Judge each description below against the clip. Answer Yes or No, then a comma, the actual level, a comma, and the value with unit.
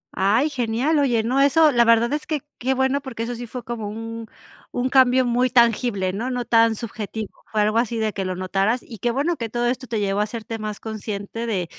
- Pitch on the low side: No, high, 230 Hz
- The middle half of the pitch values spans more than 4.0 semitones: No, average, 2.8 semitones